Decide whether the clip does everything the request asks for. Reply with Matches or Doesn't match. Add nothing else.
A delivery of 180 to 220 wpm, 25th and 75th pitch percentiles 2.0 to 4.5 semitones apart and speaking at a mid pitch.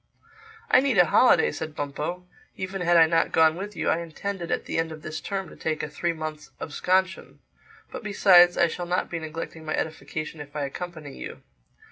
Matches